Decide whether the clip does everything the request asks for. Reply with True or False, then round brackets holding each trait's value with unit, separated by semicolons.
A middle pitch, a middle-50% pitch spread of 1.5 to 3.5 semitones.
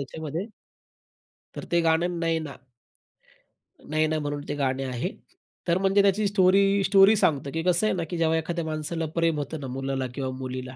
False (160 Hz; 4.2 semitones)